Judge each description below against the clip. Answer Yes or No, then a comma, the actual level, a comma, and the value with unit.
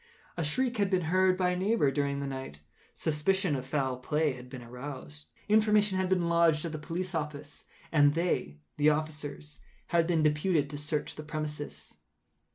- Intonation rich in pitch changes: No, average, 3.9 semitones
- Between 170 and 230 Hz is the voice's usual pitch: No, medium, 155 Hz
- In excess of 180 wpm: No, average, 175 wpm